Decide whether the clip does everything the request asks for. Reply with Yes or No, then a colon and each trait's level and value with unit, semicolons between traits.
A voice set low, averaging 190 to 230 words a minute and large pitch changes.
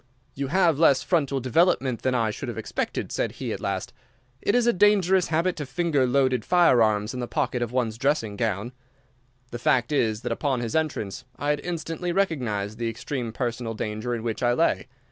Yes: low, 130 Hz; average, 195 wpm; wide, 5.7 semitones